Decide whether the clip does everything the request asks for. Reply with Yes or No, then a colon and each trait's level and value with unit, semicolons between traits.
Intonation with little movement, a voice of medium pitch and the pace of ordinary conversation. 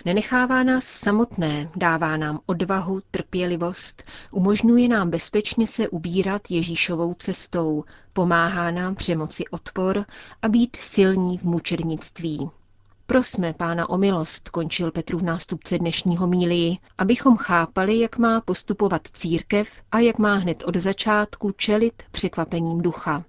No: average, 3.6 semitones; medium, 180 Hz; average, 125 wpm